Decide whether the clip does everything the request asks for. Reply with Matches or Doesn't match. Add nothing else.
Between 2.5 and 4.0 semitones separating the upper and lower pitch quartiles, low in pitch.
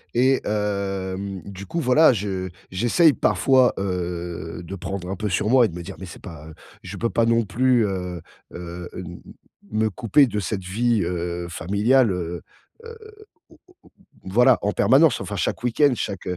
Doesn't match